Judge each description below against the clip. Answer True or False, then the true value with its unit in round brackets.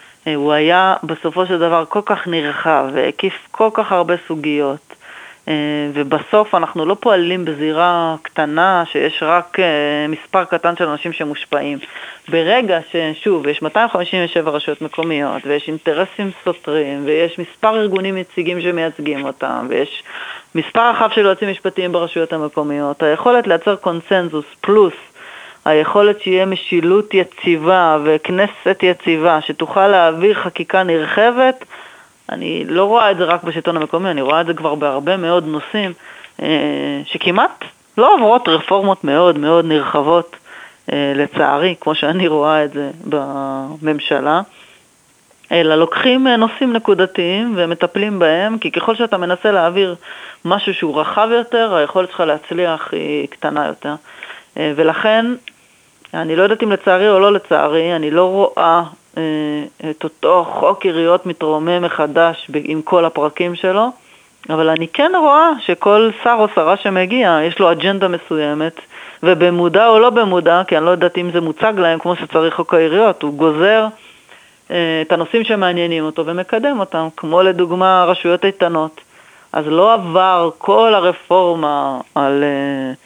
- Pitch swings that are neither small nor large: True (3.7 semitones)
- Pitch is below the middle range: False (175 Hz)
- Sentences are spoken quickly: False (135 wpm)